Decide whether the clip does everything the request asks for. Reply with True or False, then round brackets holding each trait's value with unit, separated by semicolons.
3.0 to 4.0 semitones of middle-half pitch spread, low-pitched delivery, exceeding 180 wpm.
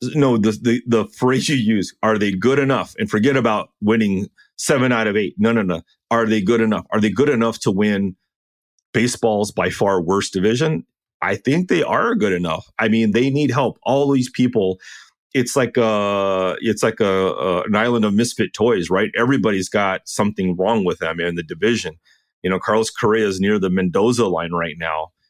True (3.6 semitones; 105 Hz; 200 wpm)